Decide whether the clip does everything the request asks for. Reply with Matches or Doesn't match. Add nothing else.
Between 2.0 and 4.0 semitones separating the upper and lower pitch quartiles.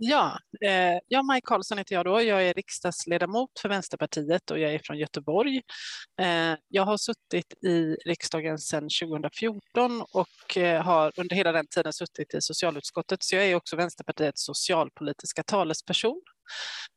Doesn't match